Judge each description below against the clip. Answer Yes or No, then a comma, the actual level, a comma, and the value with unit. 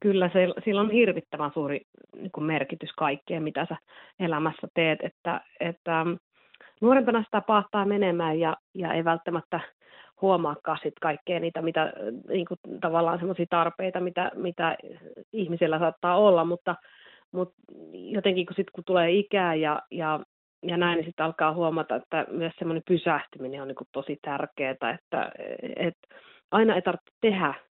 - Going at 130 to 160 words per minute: Yes, average, 140 wpm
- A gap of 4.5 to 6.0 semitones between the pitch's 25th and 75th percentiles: No, average, 2.8 semitones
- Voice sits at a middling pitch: Yes, medium, 170 Hz